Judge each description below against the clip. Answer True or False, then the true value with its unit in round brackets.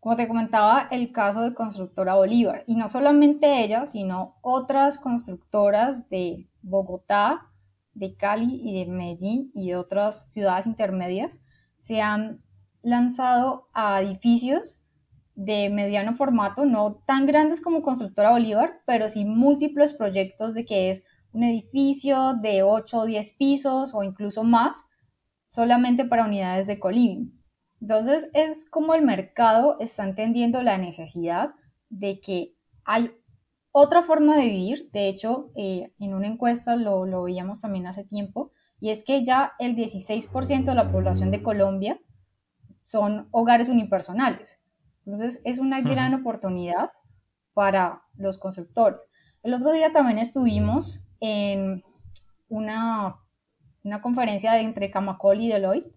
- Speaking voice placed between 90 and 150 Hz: False (220 Hz)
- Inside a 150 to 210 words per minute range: False (135 wpm)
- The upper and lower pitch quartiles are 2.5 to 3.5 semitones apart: False (4.3 semitones)